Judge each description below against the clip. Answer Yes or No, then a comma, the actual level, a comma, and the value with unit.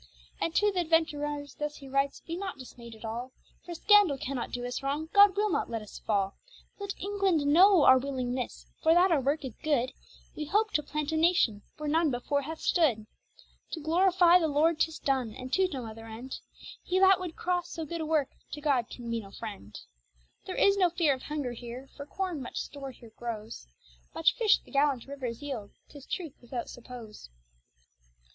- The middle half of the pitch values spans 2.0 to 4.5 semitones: No, wide, 5.4 semitones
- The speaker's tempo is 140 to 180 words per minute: No, average, 200 wpm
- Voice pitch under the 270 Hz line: No, very high, 290 Hz